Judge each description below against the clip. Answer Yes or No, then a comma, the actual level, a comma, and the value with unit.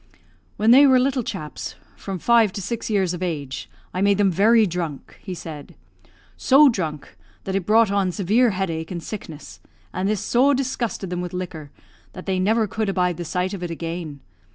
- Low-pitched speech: No, high, 190 Hz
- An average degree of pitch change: Yes, average, 4.2 semitones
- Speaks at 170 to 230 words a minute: Yes, average, 190 wpm